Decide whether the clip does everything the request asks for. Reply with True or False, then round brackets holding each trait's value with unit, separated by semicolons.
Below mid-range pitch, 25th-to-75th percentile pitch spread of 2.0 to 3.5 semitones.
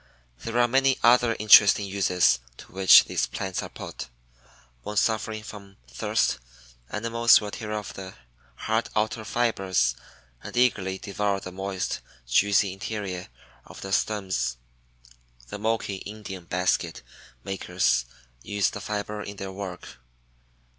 True (100 Hz; 2.5 semitones)